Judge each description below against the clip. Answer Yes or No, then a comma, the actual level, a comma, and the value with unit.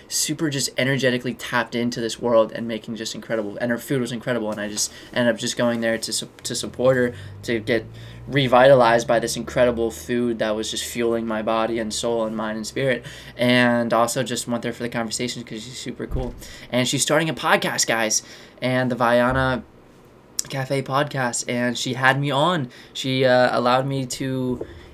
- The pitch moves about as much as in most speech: No, narrow, 2.1 semitones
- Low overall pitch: Yes, low, 120 Hz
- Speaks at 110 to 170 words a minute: No, average, 195 wpm